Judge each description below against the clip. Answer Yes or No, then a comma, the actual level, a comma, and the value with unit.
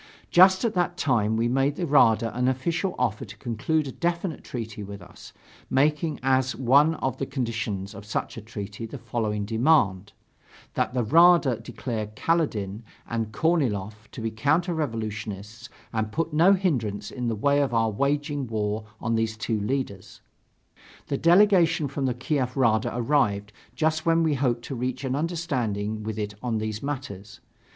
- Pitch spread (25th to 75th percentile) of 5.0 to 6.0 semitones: Yes, average, 5.3 semitones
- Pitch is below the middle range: Yes, low, 125 Hz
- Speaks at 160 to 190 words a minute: Yes, average, 165 wpm